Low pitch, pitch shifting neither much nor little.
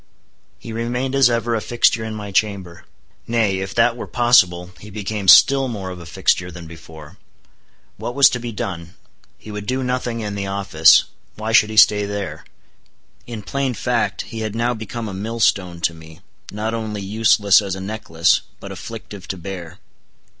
Yes: low, 105 Hz; average, 3.5 semitones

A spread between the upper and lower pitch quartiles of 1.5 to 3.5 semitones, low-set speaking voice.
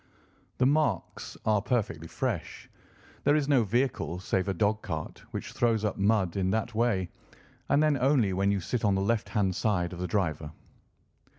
No: average, 4.3 semitones; low, 105 Hz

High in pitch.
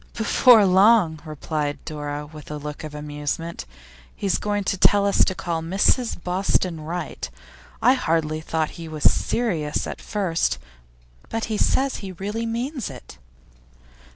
No: medium, 170 Hz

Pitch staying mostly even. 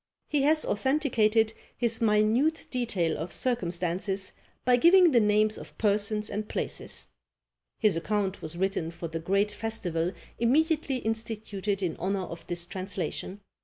No: average, 4.1 semitones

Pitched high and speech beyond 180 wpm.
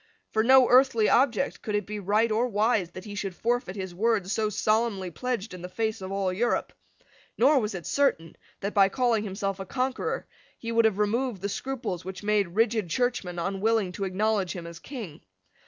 Yes: high, 210 Hz; average, 195 wpm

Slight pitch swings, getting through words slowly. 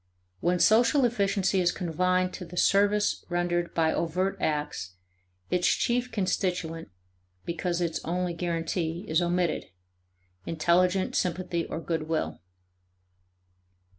Yes: narrow, 1.9 semitones; slow, 110 wpm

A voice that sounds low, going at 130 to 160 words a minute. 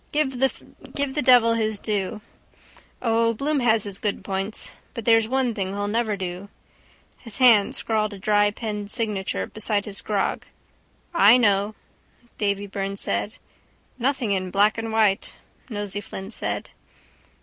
No: high, 215 Hz; average, 140 wpm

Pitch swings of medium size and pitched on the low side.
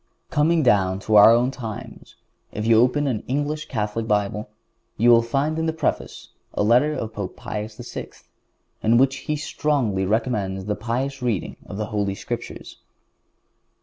Yes: average, 4.7 semitones; low, 115 Hz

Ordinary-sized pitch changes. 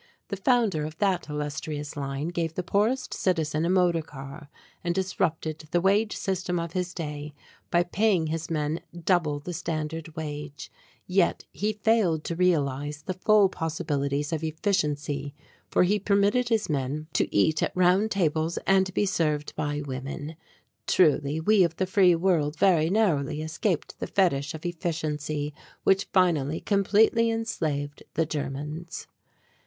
Yes: average, 4.1 semitones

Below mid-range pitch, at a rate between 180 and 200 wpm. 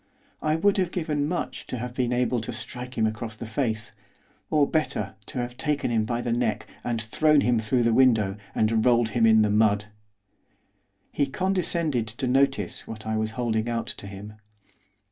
Yes: low, 120 Hz; average, 185 wpm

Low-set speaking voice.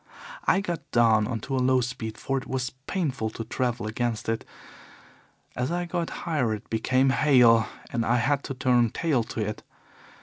Yes: low, 125 Hz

